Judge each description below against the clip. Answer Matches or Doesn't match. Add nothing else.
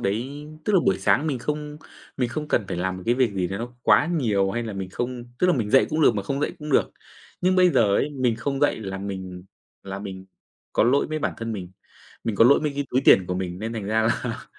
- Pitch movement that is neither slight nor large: Doesn't match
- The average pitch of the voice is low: Matches